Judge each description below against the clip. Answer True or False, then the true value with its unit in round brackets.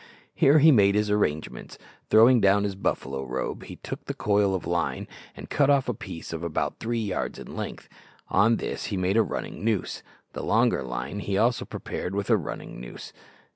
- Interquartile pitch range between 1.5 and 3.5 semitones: False (4.2 semitones)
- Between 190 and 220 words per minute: True (195 wpm)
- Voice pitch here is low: True (100 Hz)